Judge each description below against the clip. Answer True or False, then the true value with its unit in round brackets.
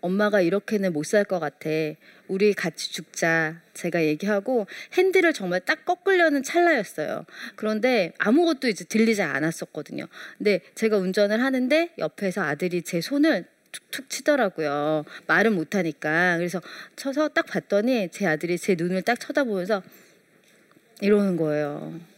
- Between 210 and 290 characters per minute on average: False (315 characters per minute)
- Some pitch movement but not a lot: False (6.2 semitones)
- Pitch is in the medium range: False (200 Hz)